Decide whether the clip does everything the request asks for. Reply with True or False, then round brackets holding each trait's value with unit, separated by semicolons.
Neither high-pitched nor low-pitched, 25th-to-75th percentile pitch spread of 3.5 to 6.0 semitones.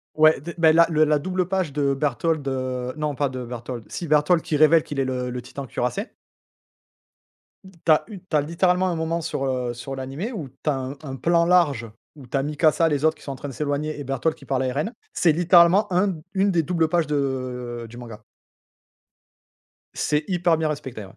True (150 Hz; 4.1 semitones)